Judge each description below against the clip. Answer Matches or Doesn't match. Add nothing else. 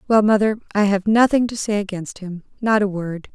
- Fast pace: Doesn't match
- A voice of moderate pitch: Doesn't match